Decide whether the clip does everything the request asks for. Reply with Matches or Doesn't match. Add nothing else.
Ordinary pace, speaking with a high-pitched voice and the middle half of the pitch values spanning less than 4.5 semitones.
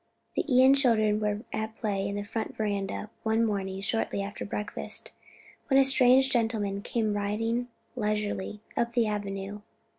Matches